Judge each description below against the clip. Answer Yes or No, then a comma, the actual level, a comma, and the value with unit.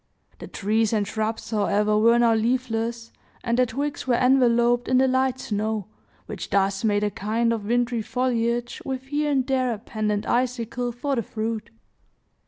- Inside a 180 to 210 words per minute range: No, average, 170 wpm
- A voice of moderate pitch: No, high, 235 Hz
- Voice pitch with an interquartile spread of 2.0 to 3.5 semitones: Yes, narrow, 2.6 semitones